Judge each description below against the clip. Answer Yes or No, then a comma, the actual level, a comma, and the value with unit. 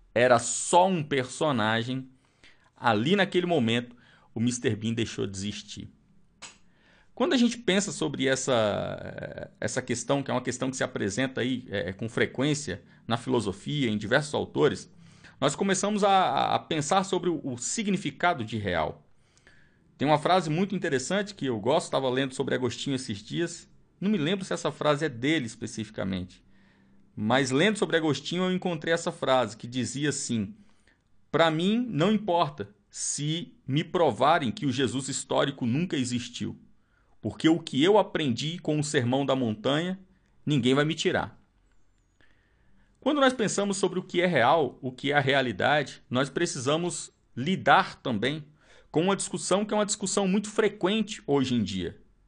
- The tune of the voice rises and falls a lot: Yes, wide, 6.8 semitones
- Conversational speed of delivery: Yes, average, 155 wpm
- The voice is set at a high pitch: No, medium, 140 Hz